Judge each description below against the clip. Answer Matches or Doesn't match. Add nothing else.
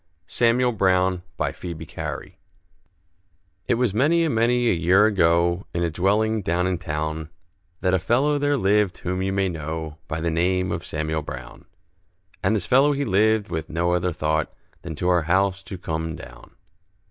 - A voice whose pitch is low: Matches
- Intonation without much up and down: Doesn't match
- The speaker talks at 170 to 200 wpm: Matches